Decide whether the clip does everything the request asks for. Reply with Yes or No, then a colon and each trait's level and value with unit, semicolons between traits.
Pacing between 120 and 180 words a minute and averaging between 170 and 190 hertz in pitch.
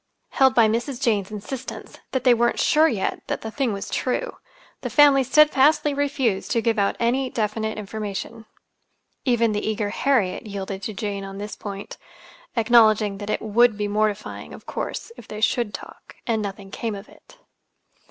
No: average, 170 wpm; high, 220 Hz